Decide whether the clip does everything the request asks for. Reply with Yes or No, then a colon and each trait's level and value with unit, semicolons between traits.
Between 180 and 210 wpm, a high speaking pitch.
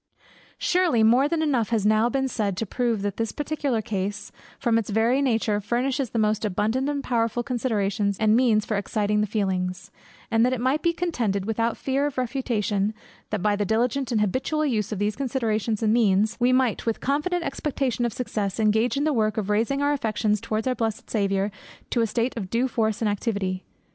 Yes: average, 200 wpm; high, 225 Hz